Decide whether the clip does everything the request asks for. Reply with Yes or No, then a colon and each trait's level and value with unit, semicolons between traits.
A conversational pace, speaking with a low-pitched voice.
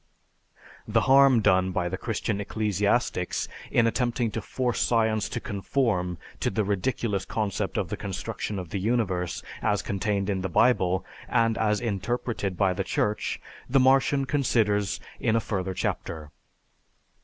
Yes: average, 145 wpm; low, 105 Hz